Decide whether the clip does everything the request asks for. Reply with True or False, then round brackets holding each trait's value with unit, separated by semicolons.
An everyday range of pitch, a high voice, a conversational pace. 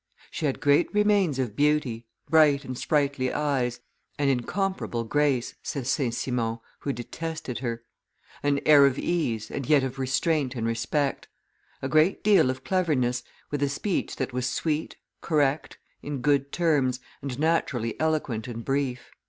False (3.4 semitones; 140 Hz; 150 wpm)